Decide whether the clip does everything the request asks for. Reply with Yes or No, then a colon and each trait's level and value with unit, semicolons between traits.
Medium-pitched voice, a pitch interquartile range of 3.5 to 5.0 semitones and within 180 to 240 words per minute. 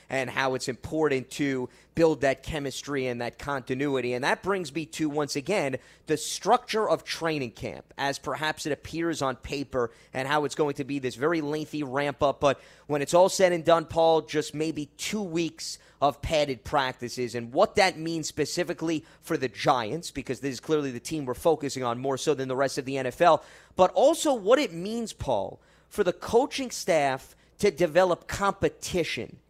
Yes: medium, 150 Hz; average, 3.9 semitones; average, 190 wpm